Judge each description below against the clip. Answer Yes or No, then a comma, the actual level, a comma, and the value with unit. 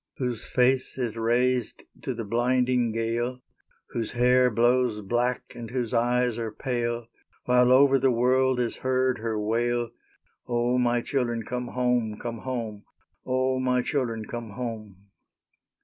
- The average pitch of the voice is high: No, low, 120 Hz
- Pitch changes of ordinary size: No, narrow, 1.5 semitones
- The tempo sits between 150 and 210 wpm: No, average, 140 wpm